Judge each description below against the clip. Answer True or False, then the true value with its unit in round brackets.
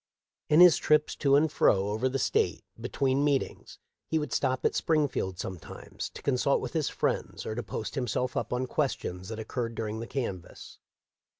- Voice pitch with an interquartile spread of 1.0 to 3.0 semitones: False (4.6 semitones)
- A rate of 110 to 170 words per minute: False (180 wpm)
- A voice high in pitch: False (130 Hz)